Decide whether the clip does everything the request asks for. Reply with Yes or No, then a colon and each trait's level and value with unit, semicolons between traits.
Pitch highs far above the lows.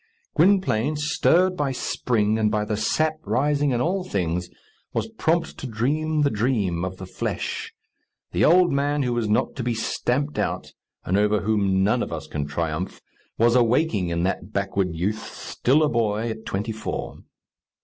Yes: wide, 6.8 semitones